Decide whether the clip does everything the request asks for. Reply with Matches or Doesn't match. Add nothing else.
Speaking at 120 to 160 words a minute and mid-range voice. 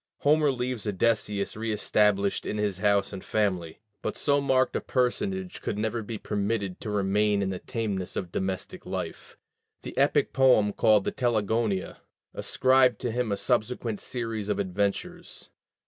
Doesn't match